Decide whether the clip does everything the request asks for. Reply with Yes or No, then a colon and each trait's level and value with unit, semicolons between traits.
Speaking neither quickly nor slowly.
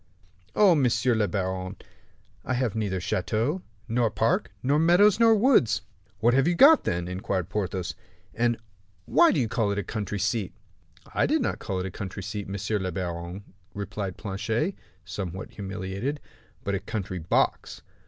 Yes: average, 165 wpm